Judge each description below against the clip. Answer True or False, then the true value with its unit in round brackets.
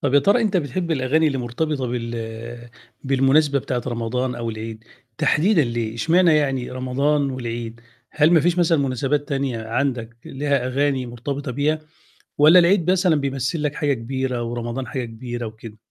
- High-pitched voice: False (135 Hz)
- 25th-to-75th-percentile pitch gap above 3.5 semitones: True (4.0 semitones)